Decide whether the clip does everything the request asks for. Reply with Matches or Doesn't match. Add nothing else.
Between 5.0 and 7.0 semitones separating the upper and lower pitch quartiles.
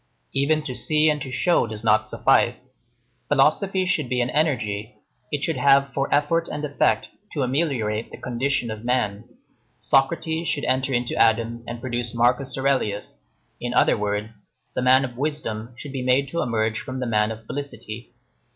Doesn't match